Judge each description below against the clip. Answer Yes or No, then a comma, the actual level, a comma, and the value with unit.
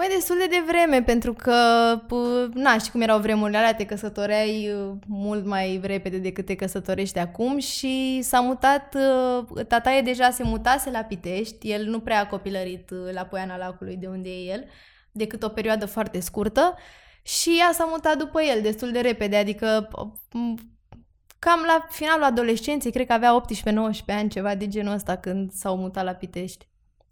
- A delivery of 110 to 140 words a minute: No, fast, 170 wpm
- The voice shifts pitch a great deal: No, average, 4.1 semitones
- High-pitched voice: Yes, high, 220 Hz